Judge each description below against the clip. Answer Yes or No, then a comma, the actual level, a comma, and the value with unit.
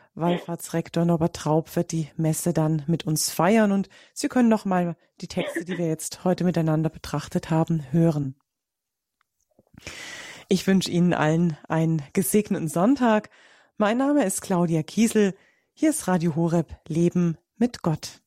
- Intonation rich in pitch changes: No, average, 3.2 semitones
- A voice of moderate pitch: Yes, medium, 170 Hz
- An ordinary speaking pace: Yes, average, 140 wpm